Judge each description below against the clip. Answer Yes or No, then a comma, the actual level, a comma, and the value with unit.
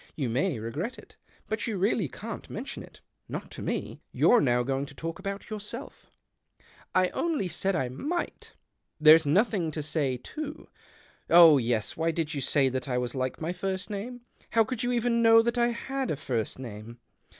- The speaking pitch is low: No, medium, 175 Hz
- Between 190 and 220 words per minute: Yes, average, 195 wpm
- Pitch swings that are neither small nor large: No, wide, 9.0 semitones